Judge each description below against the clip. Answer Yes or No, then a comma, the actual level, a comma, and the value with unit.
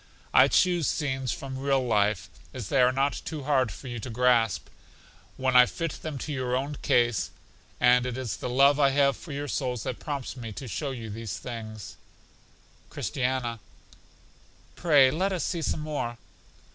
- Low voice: Yes, low, 130 Hz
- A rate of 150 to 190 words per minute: Yes, average, 175 wpm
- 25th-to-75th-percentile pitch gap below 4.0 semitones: Yes, average, 2.9 semitones